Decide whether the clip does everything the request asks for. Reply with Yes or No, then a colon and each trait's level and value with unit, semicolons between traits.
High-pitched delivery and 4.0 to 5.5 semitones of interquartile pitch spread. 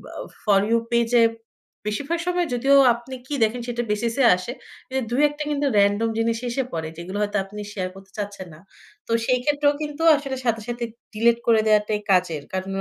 Yes: high, 230 Hz; average, 4.3 semitones